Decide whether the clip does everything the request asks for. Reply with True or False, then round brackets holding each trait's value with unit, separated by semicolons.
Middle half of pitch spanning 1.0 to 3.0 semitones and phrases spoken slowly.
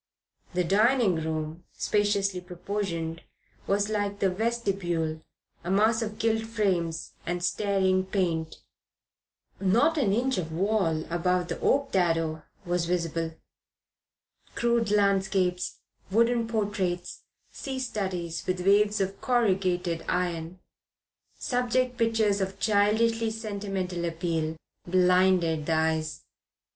False (3.8 semitones; 110 wpm)